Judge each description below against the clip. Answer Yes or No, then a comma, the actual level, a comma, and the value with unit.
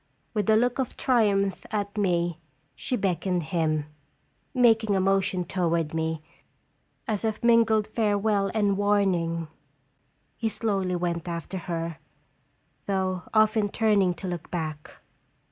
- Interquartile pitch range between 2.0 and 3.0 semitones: No, average, 3.9 semitones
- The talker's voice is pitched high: Yes, high, 195 Hz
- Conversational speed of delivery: No, slow, 125 wpm